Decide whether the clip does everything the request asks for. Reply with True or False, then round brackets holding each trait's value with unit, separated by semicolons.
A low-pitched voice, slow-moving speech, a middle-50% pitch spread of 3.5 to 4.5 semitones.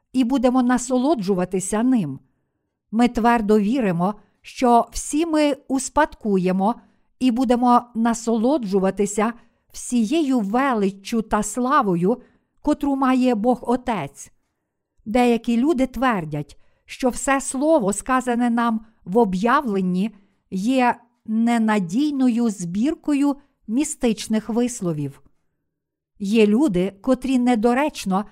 False (235 Hz; 85 wpm; 4.0 semitones)